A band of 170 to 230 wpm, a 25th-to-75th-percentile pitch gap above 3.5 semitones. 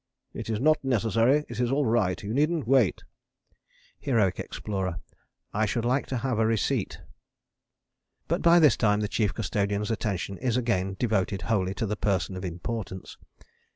No: average, 160 wpm; average, 4.1 semitones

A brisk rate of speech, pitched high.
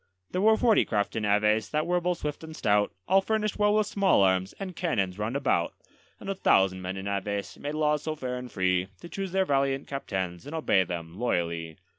No: fast, 215 wpm; low, 125 Hz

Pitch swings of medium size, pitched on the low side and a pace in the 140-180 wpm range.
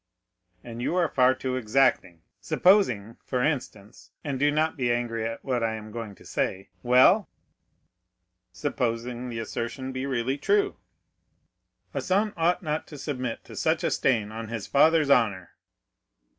Yes: average, 4.2 semitones; low, 125 Hz; average, 155 wpm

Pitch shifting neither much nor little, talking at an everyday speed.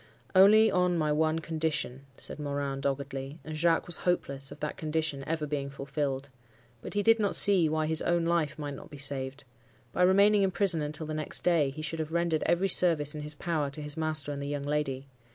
No: average, 3.1 semitones; fast, 215 wpm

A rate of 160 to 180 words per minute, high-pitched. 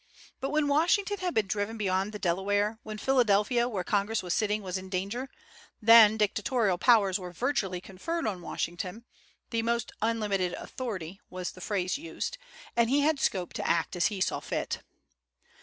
Yes: average, 170 wpm; high, 210 Hz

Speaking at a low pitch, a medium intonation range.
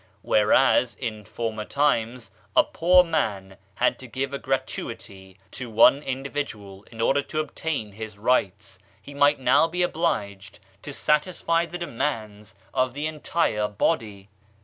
No: low, 125 Hz; wide, 5.8 semitones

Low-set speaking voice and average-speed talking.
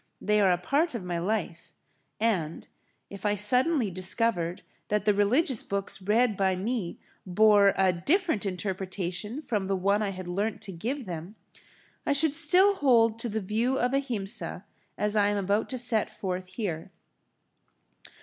No: high, 205 Hz; average, 160 wpm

